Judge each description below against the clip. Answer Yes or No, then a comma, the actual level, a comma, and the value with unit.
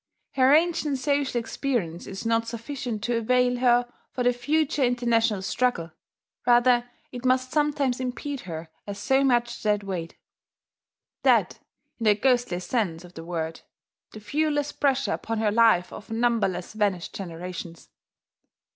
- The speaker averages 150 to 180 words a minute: No, average, 140 wpm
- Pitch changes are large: No, average, 4.4 semitones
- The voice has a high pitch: Yes, high, 240 Hz